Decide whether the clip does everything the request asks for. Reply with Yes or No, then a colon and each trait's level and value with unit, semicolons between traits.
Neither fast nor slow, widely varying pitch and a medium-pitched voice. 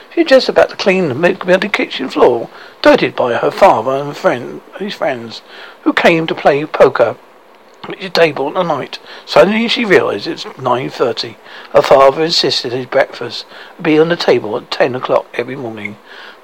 Yes: average, 175 wpm; wide, 5.8 semitones; medium, 170 Hz